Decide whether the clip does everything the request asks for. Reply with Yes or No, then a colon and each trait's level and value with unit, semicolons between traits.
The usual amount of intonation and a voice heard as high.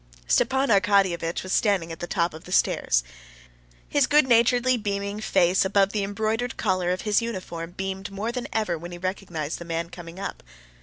Yes: average, 3.9 semitones; high, 195 Hz